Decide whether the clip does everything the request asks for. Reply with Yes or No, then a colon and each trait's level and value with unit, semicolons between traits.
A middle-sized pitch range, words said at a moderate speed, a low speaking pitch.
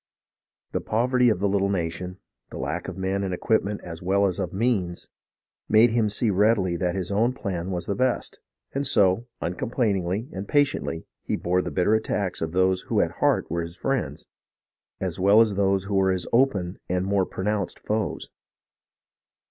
Yes: average, 3.2 semitones; average, 175 wpm; low, 100 Hz